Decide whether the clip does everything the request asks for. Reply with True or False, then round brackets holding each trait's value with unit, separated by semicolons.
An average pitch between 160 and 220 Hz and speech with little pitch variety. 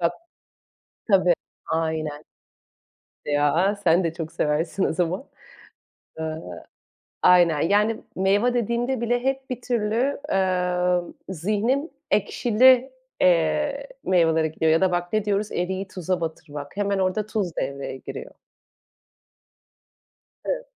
False (185 Hz; 5.1 semitones)